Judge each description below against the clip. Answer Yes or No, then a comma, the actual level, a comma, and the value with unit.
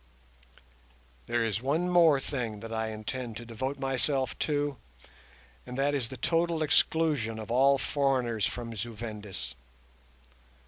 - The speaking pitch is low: Yes, low, 125 Hz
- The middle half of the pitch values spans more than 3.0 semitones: Yes, average, 4.0 semitones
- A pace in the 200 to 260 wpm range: No, slow, 135 wpm